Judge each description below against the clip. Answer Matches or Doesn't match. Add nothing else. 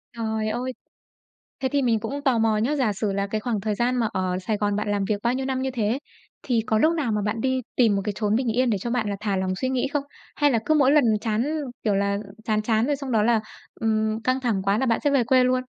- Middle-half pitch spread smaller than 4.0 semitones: Matches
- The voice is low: Doesn't match